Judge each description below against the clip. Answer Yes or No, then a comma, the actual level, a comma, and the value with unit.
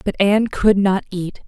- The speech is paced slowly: No, fast, 205 wpm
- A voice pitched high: Yes, high, 200 Hz